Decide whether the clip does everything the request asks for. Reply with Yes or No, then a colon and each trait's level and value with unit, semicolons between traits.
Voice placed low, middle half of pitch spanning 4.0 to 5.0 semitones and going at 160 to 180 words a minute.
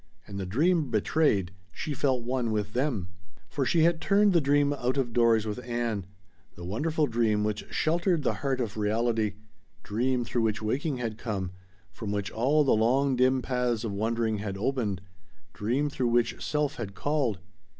Yes: low, 120 Hz; average, 4.6 semitones; average, 175 wpm